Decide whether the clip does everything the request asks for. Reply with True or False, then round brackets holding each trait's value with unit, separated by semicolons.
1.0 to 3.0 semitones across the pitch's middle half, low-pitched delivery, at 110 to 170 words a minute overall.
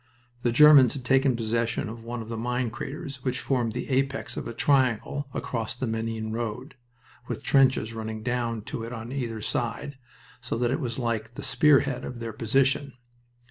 False (2.7 semitones; 120 Hz; 185 wpm)